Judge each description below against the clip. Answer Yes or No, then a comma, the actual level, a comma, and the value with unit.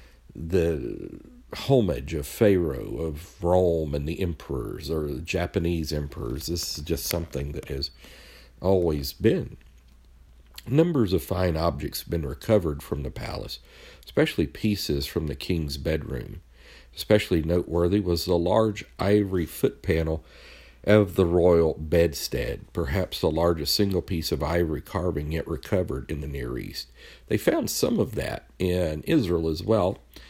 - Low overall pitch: Yes, very low, 85 Hz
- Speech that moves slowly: No, average, 145 wpm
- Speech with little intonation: No, average, 4.3 semitones